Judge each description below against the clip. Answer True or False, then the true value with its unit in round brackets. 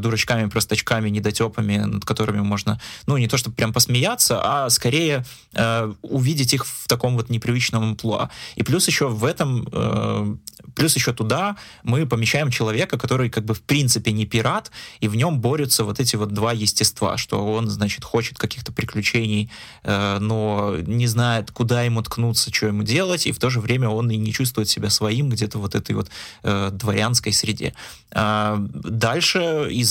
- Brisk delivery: True (175 wpm)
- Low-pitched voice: True (115 Hz)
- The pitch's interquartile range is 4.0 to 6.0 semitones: False (2.7 semitones)